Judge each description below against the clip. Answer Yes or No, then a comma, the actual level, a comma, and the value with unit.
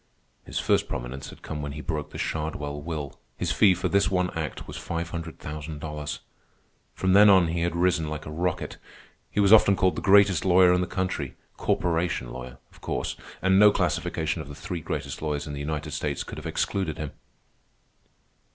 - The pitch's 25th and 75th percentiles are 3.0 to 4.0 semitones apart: Yes, average, 3.4 semitones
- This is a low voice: Yes, very low, 80 Hz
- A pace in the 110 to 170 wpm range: No, average, 195 wpm